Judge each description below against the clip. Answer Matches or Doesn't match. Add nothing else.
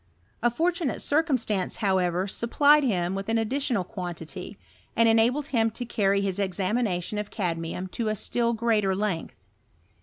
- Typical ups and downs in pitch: Matches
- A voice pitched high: Matches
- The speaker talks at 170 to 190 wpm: Doesn't match